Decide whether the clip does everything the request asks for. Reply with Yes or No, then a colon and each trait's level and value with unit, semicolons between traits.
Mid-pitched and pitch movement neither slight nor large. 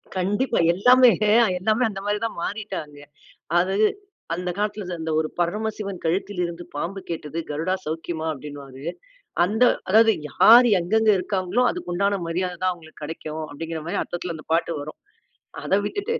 Yes: medium, 180 Hz; average, 4.3 semitones